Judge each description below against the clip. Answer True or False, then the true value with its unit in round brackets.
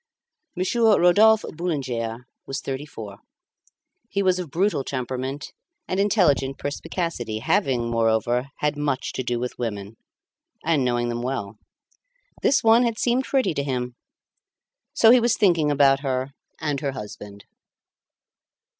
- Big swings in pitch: True (6.8 semitones)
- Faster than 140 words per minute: False (135 wpm)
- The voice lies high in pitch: False (140 Hz)